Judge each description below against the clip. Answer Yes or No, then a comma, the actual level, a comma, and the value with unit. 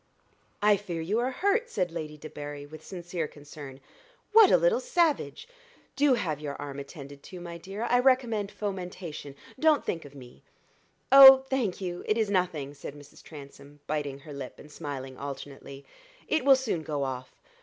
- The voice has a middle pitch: Yes, medium, 165 Hz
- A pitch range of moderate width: No, wide, 7.9 semitones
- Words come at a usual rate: Yes, average, 170 wpm